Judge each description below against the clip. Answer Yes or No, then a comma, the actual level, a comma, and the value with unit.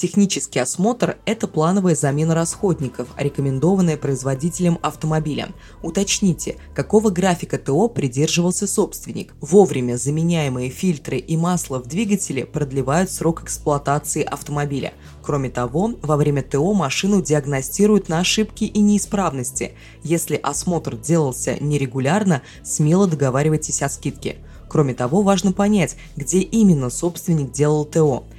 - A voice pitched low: No, medium, 155 Hz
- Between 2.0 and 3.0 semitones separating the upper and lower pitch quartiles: No, average, 5.0 semitones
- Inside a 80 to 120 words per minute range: Yes, average, 115 wpm